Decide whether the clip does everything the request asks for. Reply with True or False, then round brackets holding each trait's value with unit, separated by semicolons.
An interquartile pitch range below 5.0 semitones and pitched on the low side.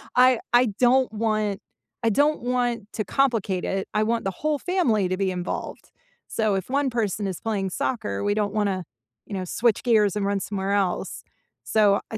False (3.8 semitones; 215 Hz)